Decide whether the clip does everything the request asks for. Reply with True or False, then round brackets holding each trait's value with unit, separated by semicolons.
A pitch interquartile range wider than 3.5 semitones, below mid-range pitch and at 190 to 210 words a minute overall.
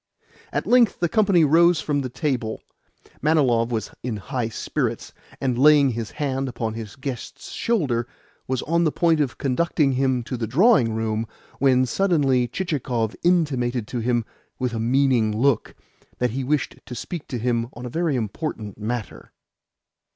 False (4.4 semitones; 130 Hz; 160 wpm)